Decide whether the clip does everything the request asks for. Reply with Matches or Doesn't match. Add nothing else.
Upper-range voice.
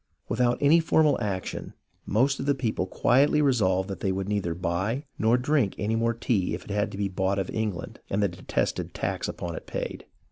Doesn't match